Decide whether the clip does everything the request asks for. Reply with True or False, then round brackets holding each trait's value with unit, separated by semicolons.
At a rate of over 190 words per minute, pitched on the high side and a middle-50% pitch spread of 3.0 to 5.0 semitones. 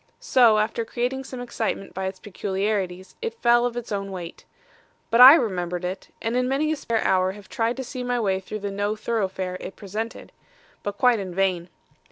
True (200 wpm; 215 Hz; 4.1 semitones)